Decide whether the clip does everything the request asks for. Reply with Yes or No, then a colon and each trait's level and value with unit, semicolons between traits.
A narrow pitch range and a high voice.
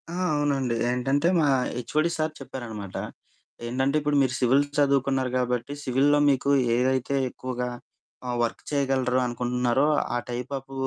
No: narrow, 2.2 semitones; low, 130 Hz